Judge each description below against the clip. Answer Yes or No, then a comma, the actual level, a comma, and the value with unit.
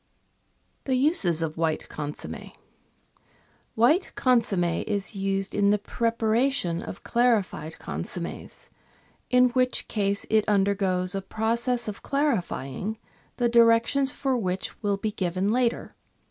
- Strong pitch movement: No, average, 4.1 semitones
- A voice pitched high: Yes, high, 215 Hz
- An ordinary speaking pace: No, slow, 120 wpm